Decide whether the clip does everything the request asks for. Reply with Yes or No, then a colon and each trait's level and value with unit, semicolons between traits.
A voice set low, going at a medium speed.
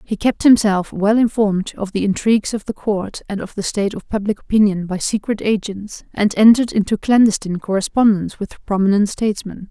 No: high, 205 Hz; average, 180 wpm